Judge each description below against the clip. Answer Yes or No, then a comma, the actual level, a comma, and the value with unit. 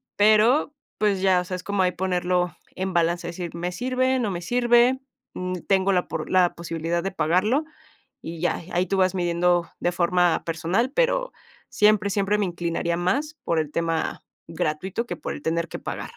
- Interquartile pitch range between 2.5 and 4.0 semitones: Yes, average, 3.4 semitones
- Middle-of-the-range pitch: Yes, medium, 180 Hz